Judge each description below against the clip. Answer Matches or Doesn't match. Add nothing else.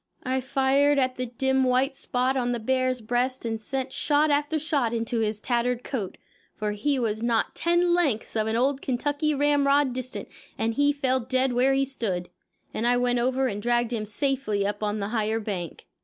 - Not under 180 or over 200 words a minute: Matches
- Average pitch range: Matches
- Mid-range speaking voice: Doesn't match